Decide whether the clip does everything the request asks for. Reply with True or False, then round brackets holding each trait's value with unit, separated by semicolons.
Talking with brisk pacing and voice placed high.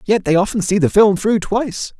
True (240 wpm; 200 Hz)